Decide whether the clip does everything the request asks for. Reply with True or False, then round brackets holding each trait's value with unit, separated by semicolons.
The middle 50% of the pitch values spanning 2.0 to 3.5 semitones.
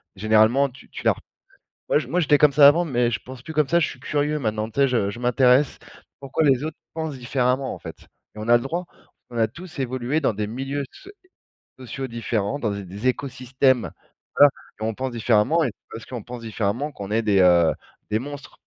False (4.1 semitones)